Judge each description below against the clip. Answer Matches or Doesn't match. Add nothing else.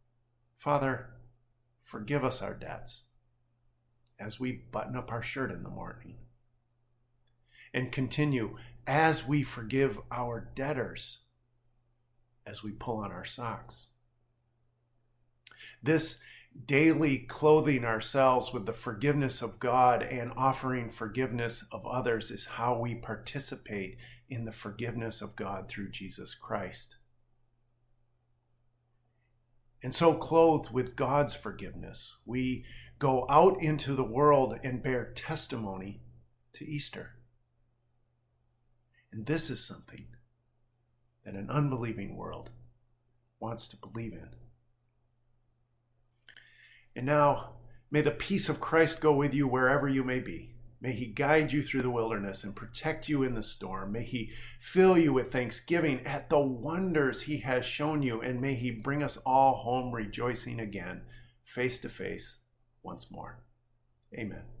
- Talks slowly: Matches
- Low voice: Matches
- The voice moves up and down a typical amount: Doesn't match